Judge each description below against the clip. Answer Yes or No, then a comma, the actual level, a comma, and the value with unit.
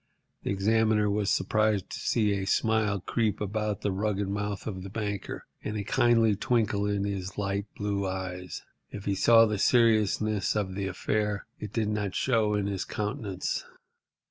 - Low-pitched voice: Yes, low, 105 Hz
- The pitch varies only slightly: Yes, narrow, 1.6 semitones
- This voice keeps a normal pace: Yes, average, 170 wpm